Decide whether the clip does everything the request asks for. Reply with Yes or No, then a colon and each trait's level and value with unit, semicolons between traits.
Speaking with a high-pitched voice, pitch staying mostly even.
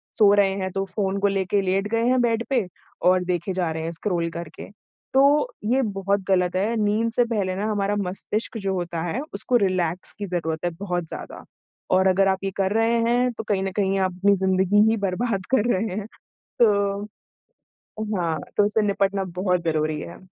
Yes: high, 195 Hz; narrow, 2.3 semitones